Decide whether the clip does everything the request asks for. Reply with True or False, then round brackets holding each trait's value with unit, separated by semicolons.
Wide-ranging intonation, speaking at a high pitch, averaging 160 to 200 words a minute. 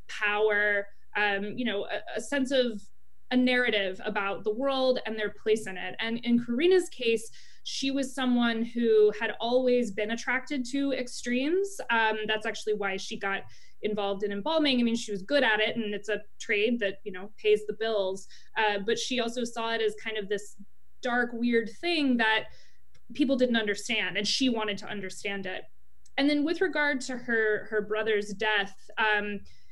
False (3.2 semitones; 220 Hz; 185 wpm)